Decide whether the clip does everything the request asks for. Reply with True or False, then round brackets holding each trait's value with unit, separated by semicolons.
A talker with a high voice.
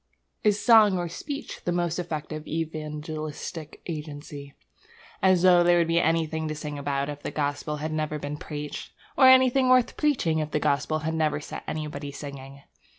False (155 Hz)